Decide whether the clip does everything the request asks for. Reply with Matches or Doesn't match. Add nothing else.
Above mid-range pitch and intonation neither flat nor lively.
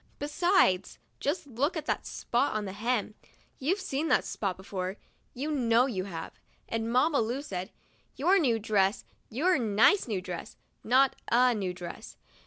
Doesn't match